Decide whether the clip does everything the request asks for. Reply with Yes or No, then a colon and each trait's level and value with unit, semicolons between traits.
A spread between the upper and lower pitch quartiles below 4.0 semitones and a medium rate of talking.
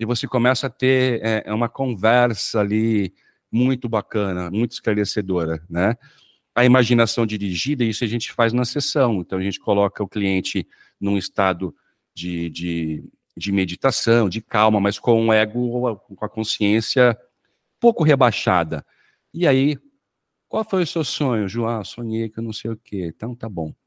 Yes: average, 3.6 semitones; average, 160 wpm